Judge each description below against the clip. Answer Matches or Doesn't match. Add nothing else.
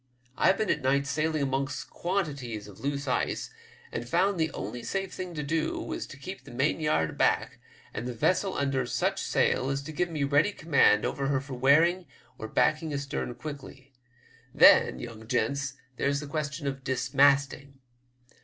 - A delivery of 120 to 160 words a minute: Doesn't match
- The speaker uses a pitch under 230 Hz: Matches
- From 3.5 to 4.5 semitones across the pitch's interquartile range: Doesn't match